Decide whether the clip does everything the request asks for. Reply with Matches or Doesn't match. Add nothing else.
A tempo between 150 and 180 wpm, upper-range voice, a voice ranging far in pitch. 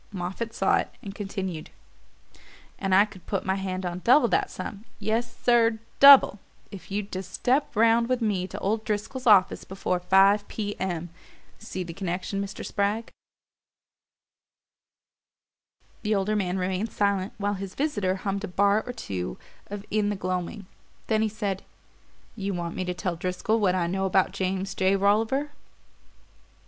Doesn't match